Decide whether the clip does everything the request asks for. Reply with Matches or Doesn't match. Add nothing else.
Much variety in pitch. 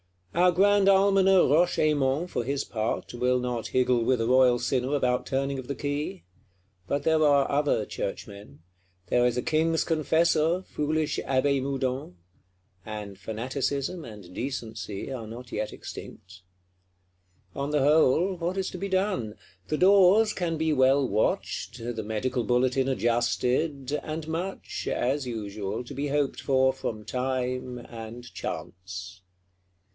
Doesn't match